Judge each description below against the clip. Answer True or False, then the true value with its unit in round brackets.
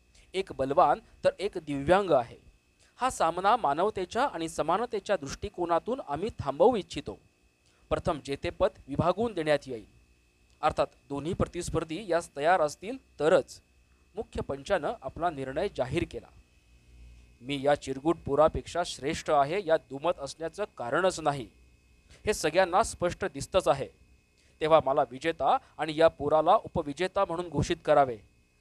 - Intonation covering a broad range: False (5.0 semitones)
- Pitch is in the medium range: True (155 Hz)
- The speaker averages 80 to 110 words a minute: False (125 wpm)